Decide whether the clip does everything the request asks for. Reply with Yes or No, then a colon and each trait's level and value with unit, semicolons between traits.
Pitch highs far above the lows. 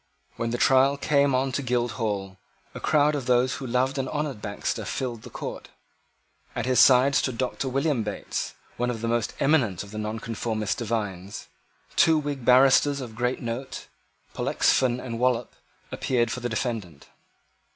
No: average, 2.9 semitones